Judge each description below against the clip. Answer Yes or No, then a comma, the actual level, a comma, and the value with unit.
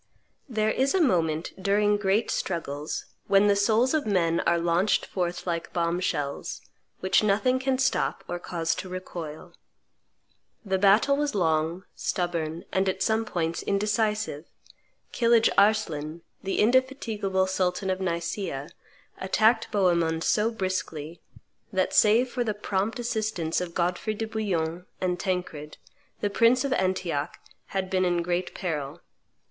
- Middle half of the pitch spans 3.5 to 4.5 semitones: Yes, average, 4.1 semitones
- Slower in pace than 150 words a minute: Yes, average, 140 wpm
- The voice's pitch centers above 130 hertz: Yes, high, 190 Hz